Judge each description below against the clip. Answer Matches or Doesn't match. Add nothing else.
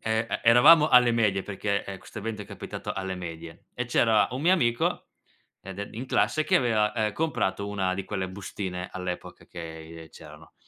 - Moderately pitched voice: Doesn't match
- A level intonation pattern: Doesn't match